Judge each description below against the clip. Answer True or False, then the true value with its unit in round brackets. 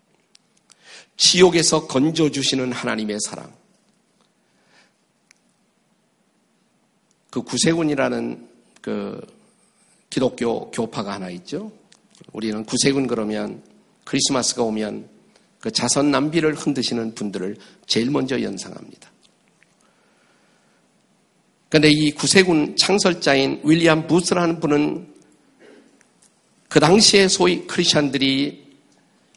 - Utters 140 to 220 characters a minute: True (215 characters per minute)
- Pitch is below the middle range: False (160 Hz)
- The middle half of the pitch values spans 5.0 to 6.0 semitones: False (7.1 semitones)